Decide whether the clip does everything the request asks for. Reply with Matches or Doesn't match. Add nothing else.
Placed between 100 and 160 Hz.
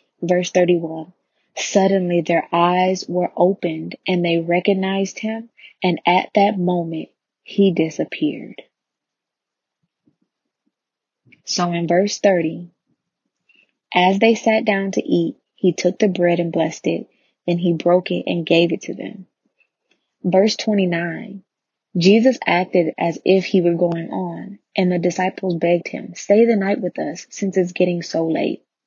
Doesn't match